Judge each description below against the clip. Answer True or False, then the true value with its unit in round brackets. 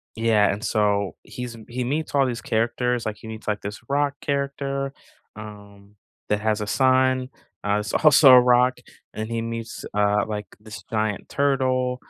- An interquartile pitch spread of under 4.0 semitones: True (3.6 semitones)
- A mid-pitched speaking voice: False (115 Hz)